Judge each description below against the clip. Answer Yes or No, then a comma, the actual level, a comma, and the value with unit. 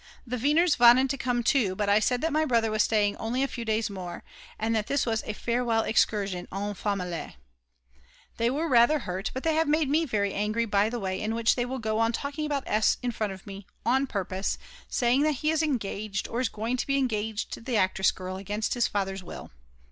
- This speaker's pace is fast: Yes, fast, 230 wpm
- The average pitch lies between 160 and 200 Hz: No, high, 225 Hz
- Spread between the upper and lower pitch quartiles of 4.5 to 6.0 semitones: No, average, 4.1 semitones